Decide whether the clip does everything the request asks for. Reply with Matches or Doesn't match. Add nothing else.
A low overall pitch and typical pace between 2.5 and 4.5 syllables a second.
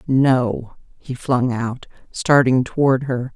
Matches